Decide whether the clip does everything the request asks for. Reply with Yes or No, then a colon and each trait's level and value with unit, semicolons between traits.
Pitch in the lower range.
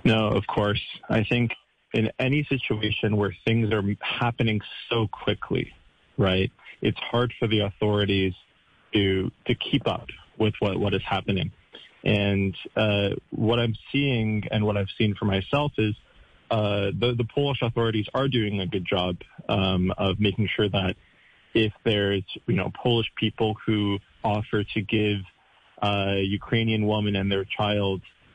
Yes: low, 105 Hz